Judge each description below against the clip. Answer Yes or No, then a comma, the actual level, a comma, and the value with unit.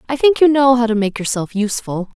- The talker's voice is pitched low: No, high, 235 Hz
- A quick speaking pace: Yes, fast, 245 wpm